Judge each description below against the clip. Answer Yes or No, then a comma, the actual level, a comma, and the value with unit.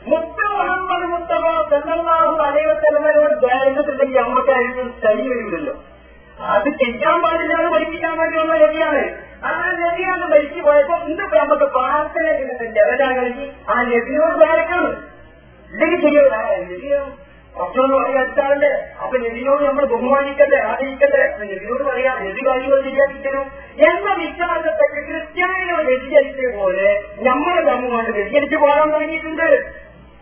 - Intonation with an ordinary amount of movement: Yes, average, 3.2 semitones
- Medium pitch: No, very high, 290 Hz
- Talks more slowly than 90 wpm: No, average, 105 wpm